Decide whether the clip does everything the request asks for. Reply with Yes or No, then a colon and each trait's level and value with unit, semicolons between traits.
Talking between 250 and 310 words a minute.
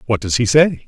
Yes: fast, 275 wpm